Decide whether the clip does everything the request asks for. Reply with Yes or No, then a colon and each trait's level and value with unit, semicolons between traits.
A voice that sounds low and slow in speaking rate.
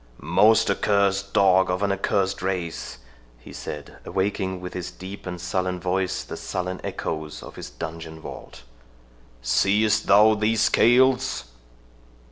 Yes: very low, 95 Hz; slow, 130 wpm